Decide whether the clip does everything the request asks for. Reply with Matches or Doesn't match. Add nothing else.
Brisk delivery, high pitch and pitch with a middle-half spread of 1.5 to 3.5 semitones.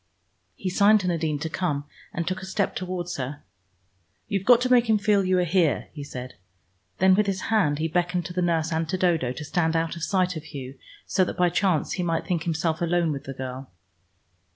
Doesn't match